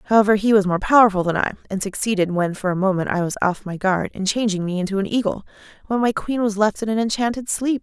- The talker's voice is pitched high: Yes, high, 205 Hz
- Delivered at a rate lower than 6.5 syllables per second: No, 6.6 syllables/s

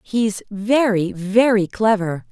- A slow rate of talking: Yes, slow, 105 wpm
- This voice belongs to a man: No, female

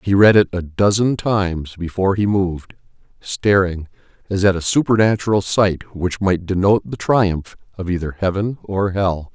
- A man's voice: Yes, male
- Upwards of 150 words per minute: Yes, average, 160 wpm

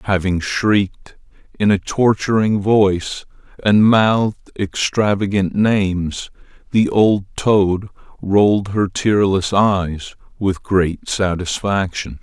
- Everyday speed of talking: No, slow, 100 wpm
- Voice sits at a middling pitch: No, low, 100 Hz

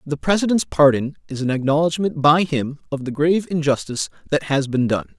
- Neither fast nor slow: Yes, average, 185 wpm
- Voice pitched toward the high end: No, medium, 150 Hz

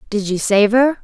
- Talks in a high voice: Yes, high, 220 Hz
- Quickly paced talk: Yes, fast, 230 wpm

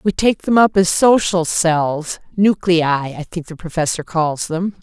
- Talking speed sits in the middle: Yes, average, 175 wpm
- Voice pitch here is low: No, medium, 175 Hz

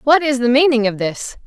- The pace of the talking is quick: Yes, fast, 245 wpm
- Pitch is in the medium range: No, very high, 255 Hz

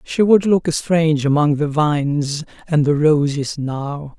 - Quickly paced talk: No, average, 160 wpm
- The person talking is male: Yes, male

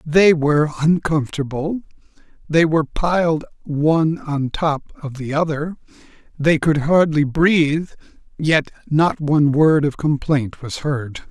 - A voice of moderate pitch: Yes, medium, 155 Hz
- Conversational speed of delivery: No, slow, 125 wpm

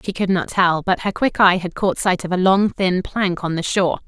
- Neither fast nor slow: No, fast, 280 wpm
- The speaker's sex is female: Yes, female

